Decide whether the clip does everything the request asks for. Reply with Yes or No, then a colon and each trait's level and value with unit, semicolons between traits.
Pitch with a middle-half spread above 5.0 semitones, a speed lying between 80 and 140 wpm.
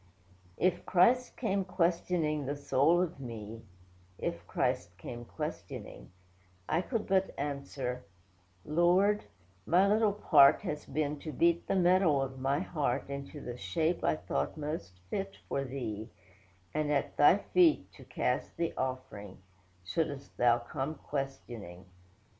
Yes: wide, 5.5 semitones; slow, 135 wpm